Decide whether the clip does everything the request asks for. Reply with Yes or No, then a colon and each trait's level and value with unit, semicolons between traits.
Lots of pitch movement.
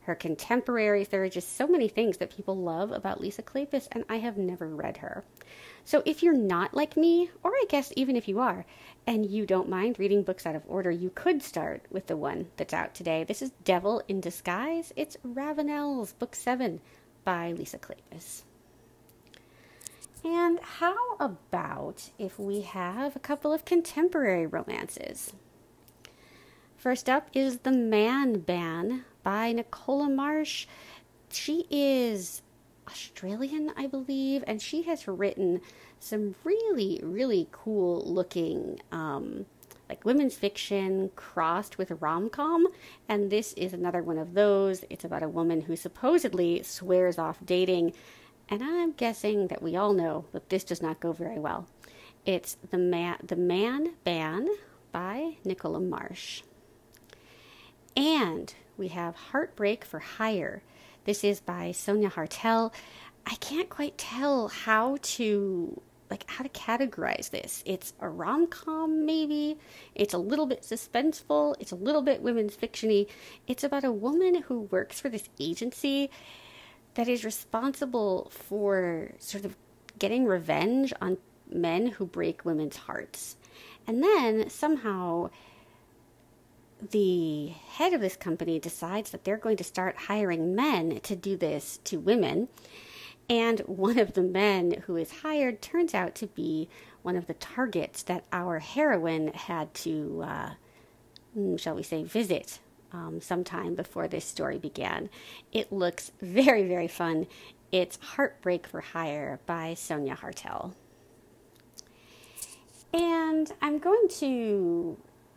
Yes: wide, 7.6 semitones